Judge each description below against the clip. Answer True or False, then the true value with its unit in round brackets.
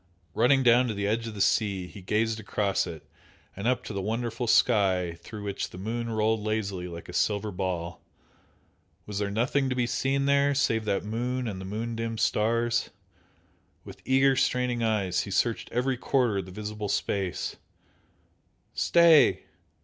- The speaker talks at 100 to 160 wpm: False (170 wpm)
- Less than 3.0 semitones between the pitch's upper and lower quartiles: False (3.4 semitones)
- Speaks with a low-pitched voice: True (110 Hz)